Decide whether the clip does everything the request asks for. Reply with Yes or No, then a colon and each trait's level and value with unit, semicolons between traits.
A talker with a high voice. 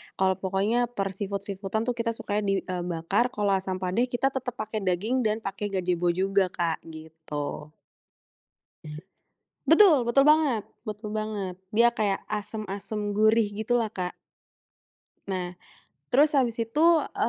Yes: high, 205 Hz